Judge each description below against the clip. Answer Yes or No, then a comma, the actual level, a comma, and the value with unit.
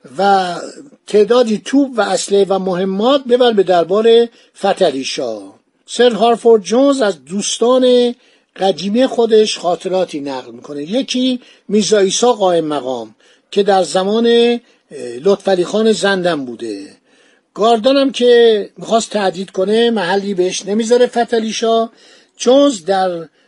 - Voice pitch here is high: Yes, high, 210 Hz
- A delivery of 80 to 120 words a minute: Yes, average, 110 wpm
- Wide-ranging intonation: No, average, 4.3 semitones